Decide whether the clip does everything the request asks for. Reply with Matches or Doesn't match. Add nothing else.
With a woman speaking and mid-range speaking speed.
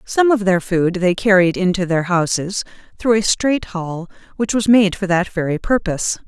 Matches